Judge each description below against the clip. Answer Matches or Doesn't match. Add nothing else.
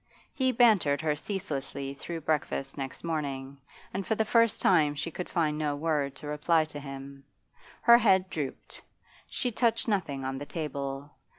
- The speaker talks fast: Doesn't match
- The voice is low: Doesn't match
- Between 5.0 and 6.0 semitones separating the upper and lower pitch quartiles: Matches